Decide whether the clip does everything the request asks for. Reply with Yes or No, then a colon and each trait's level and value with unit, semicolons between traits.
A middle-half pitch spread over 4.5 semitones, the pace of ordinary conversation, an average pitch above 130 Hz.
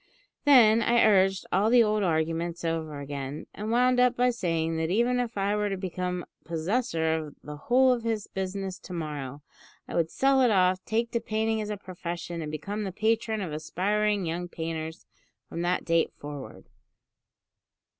Yes: average, 5.1 semitones; average, 175 wpm; high, 190 Hz